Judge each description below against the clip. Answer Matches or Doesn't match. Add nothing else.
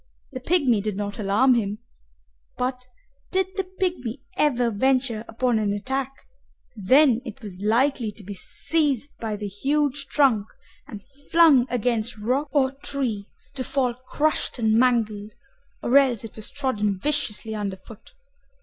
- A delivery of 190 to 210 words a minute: Doesn't match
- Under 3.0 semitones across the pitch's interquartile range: Doesn't match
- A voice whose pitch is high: Matches